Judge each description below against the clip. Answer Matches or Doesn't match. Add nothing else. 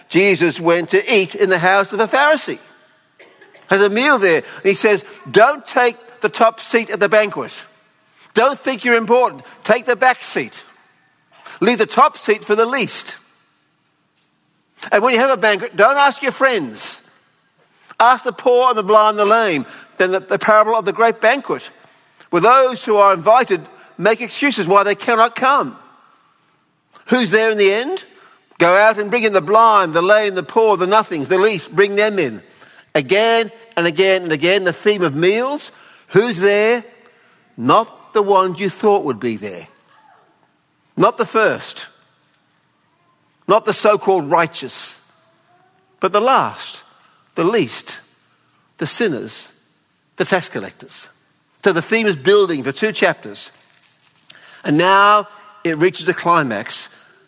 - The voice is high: Matches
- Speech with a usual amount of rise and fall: Matches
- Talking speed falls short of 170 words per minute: Matches